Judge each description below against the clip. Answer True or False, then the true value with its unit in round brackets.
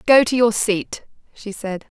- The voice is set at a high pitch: True (220 Hz)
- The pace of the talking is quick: False (180 wpm)